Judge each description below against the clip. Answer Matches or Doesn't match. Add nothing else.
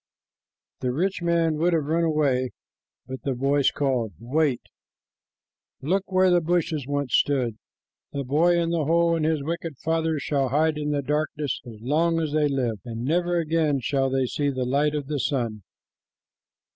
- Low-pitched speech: Doesn't match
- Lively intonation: Doesn't match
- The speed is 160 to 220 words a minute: Matches